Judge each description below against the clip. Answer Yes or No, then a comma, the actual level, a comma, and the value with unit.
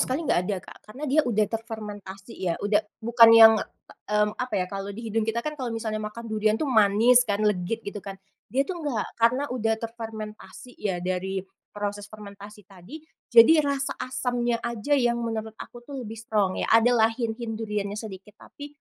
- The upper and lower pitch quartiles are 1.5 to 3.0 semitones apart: Yes, narrow, 2.5 semitones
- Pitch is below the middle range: No, high, 220 Hz